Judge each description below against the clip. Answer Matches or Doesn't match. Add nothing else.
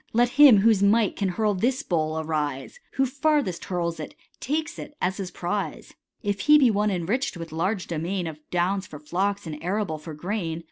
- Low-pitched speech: Doesn't match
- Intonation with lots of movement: Doesn't match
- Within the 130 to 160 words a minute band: Doesn't match